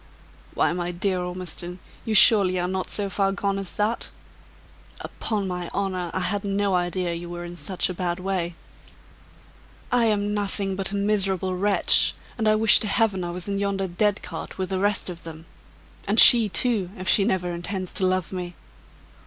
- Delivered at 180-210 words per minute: Yes, average, 185 wpm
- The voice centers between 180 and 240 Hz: Yes, high, 190 Hz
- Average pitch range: No, narrow, 2.2 semitones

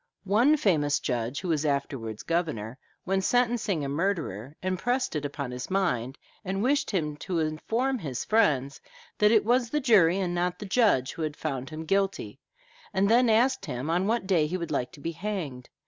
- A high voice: No, medium, 175 Hz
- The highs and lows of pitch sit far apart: Yes, wide, 6.7 semitones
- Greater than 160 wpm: Yes, average, 190 wpm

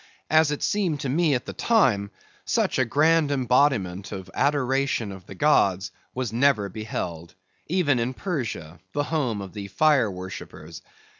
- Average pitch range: No, wide, 6.9 semitones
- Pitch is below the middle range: Yes, low, 125 Hz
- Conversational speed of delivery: Yes, average, 155 wpm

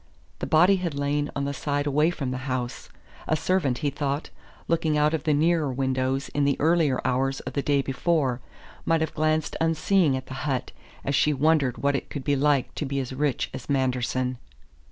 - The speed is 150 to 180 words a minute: No, average, 200 wpm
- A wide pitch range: No, average, 2.9 semitones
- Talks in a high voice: No, medium, 140 Hz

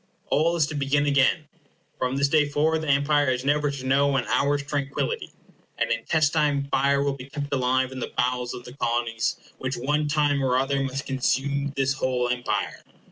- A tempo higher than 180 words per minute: Yes, average, 190 wpm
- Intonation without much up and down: Yes, narrow, 1.9 semitones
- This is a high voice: No, medium, 140 Hz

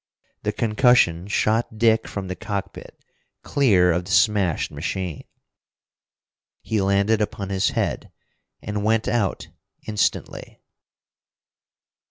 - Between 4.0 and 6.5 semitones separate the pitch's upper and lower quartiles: No, average, 2.7 semitones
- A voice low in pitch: Yes, low, 105 Hz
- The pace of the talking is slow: Yes, slow, 105 wpm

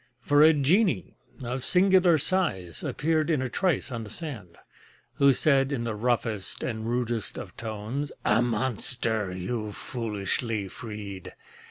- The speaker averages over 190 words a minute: No, average, 140 wpm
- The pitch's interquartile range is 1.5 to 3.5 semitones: No, average, 5.3 semitones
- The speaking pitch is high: No, low, 120 Hz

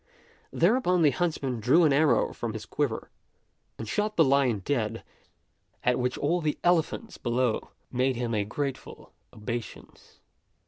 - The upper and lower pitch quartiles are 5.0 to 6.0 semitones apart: Yes, average, 5.3 semitones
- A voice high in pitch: No, low, 135 Hz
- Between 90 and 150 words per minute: Yes, average, 140 wpm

